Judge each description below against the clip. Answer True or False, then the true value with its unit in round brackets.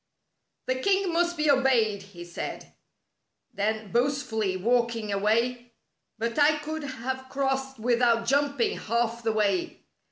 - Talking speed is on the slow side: True (130 wpm)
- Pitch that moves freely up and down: False (3.7 semitones)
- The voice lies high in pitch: True (240 Hz)